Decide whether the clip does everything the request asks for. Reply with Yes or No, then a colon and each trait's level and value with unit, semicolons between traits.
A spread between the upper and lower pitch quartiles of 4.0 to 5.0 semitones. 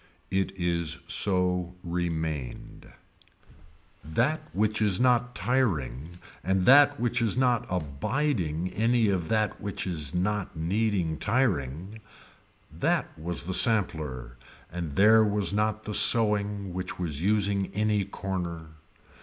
Yes: average, 4.3 semitones